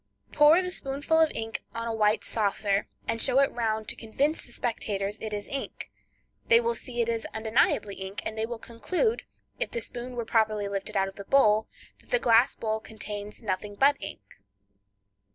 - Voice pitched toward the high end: Yes, high, 225 Hz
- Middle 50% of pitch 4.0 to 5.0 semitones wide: Yes, average, 4.3 semitones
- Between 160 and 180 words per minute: No, average, 190 wpm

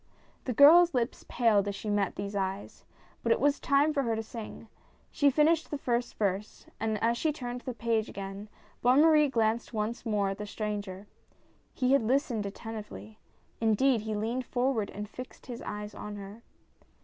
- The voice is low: No, high, 225 Hz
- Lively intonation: No, average, 3.6 semitones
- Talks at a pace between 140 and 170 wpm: No, average, 185 wpm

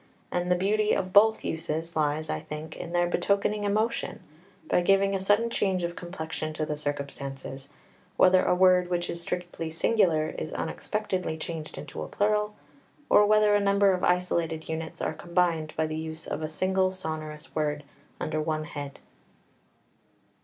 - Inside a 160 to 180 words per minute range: Yes, average, 165 wpm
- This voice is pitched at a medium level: Yes, medium, 175 Hz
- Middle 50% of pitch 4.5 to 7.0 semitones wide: No, average, 3.7 semitones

